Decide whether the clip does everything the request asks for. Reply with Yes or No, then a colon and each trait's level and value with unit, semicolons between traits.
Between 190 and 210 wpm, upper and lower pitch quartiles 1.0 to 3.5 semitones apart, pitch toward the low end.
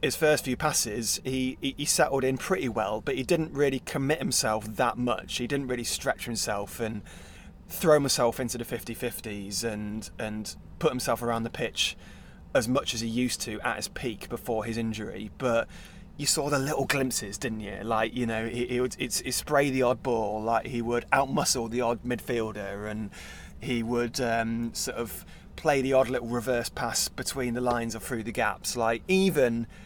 Yes: average, 195 wpm; average, 2.8 semitones; low, 120 Hz